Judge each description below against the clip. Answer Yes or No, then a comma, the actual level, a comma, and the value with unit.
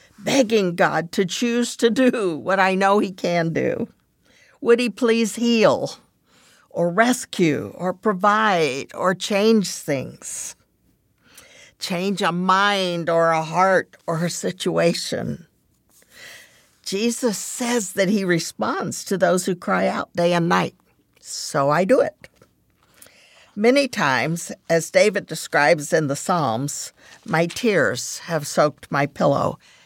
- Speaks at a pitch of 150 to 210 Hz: Yes, high, 190 Hz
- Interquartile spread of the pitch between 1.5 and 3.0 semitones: No, average, 4.7 semitones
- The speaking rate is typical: No, slow, 125 wpm